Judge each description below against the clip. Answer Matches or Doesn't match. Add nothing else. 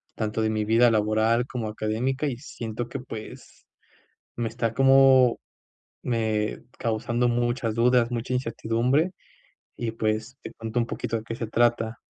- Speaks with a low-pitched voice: Matches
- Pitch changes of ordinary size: Doesn't match